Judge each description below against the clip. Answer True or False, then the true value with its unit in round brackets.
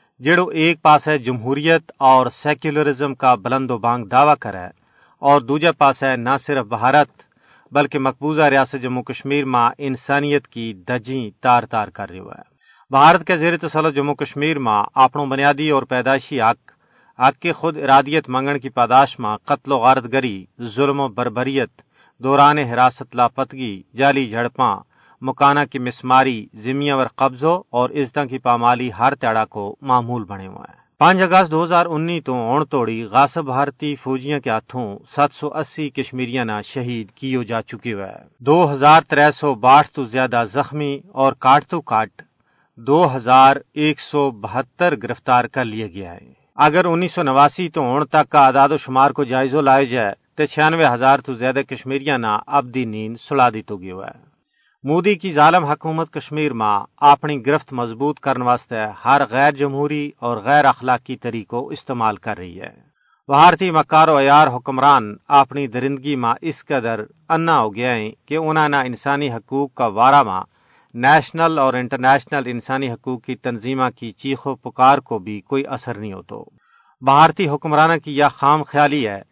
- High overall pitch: False (135 Hz)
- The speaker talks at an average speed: True (165 wpm)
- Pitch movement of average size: True (3.2 semitones)